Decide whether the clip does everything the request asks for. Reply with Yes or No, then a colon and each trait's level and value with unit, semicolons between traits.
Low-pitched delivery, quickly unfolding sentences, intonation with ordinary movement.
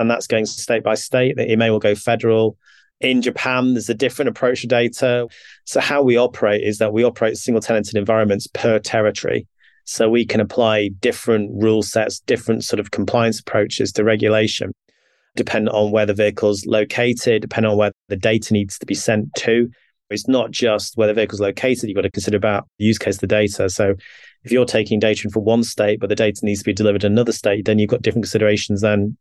No: low, 110 Hz; fast, 215 wpm; narrow, 2.0 semitones